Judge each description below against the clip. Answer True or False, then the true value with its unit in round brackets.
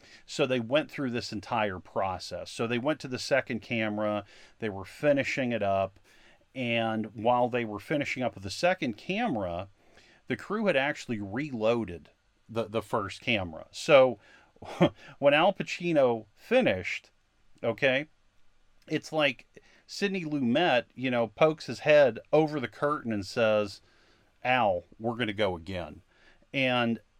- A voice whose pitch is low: True (115 Hz)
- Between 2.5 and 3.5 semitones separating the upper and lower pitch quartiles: False (4.9 semitones)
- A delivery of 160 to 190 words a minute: False (145 wpm)